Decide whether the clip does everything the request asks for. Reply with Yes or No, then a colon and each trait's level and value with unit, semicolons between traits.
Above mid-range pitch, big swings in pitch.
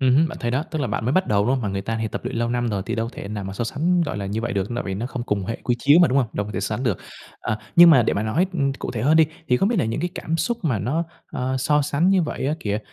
No: low, 125 Hz; wide, 5.9 semitones